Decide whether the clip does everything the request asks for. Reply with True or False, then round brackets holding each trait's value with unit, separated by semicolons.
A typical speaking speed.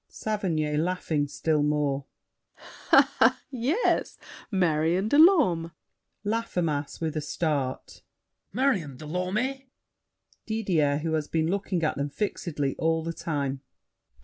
False (110 wpm)